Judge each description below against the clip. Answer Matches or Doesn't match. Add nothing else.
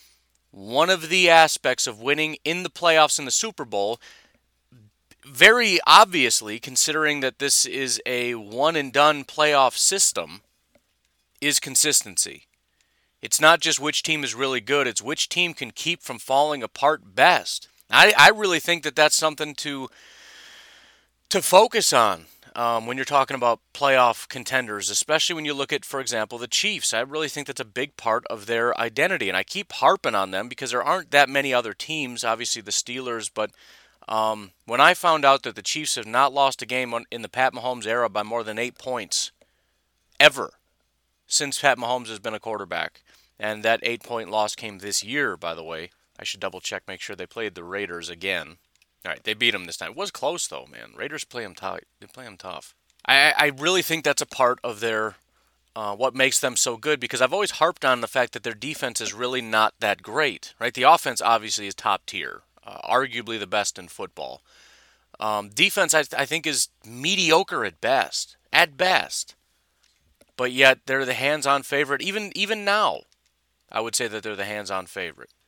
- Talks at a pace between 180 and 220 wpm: Matches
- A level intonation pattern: Doesn't match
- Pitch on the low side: Matches